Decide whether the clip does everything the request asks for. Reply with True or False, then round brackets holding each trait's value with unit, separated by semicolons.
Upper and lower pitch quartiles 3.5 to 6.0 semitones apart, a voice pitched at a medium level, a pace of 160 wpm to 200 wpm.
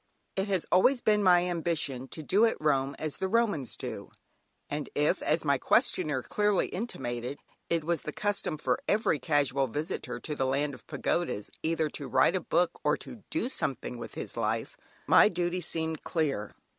True (5.0 semitones; 160 Hz; 180 wpm)